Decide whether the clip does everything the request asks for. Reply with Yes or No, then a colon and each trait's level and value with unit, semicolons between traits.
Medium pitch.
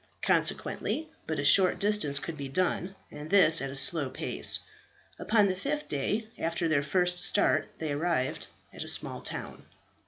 Yes: medium, 165 Hz